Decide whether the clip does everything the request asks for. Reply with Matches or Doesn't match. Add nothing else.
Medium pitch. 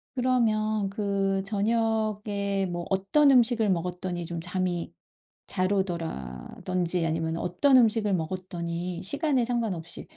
Doesn't match